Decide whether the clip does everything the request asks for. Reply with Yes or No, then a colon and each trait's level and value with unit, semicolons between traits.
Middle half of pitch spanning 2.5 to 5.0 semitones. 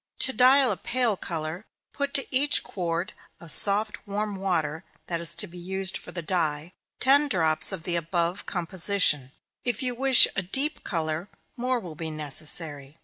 No: wide, 5.6 semitones